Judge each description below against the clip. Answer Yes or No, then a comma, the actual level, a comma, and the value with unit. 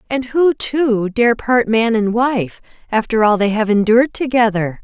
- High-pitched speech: Yes, high, 230 Hz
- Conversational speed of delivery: Yes, average, 175 wpm